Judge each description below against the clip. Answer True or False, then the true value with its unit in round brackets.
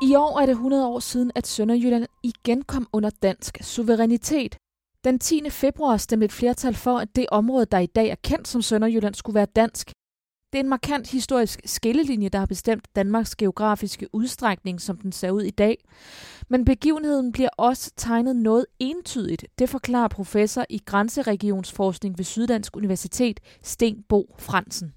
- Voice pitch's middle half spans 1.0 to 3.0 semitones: False (3.6 semitones)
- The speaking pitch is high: True (230 Hz)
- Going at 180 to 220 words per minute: False (165 wpm)